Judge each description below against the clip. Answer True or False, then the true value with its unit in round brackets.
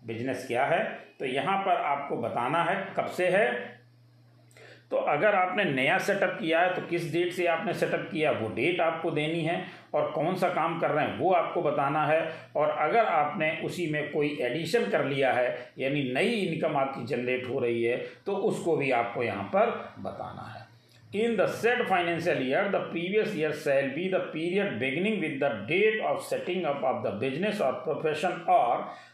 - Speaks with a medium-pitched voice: True (160 Hz)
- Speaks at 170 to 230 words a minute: True (185 wpm)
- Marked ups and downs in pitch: True (6.2 semitones)